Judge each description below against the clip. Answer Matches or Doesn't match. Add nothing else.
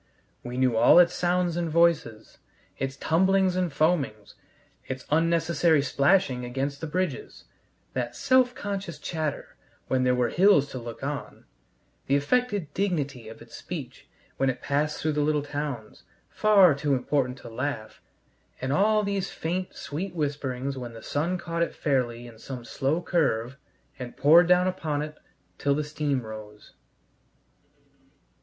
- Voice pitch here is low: Doesn't match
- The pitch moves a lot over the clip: Doesn't match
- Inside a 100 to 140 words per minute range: Doesn't match